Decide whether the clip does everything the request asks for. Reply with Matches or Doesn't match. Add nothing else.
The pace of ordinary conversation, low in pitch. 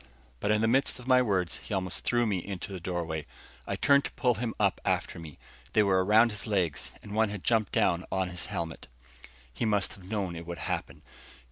Doesn't match